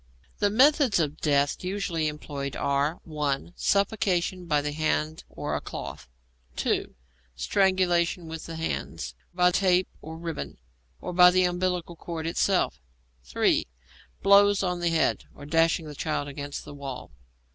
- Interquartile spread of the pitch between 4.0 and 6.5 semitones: No, average, 3.6 semitones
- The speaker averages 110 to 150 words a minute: Yes, average, 145 wpm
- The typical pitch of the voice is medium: Yes, medium, 165 Hz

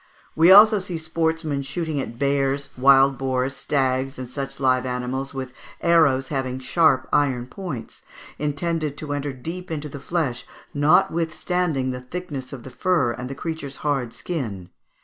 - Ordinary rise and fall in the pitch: Yes, average, 3.7 semitones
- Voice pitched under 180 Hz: Yes, medium, 140 Hz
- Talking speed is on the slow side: No, average, 155 wpm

